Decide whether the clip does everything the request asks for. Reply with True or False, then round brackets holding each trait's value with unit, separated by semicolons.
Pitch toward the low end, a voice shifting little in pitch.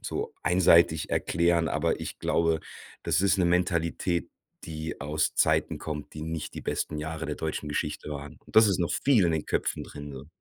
True (80 Hz; 2.2 semitones)